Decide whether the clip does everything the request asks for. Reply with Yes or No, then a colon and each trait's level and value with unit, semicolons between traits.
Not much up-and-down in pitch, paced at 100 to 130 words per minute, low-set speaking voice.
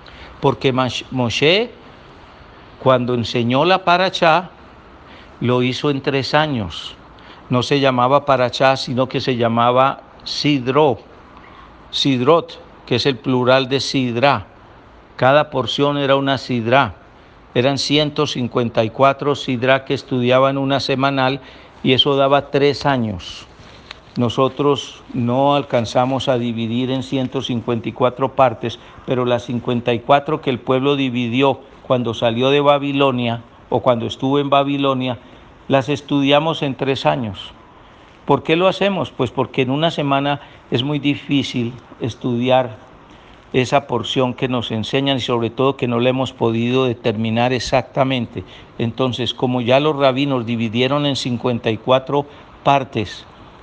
Yes: narrow, 2.3 semitones; slow, 125 wpm; low, 130 Hz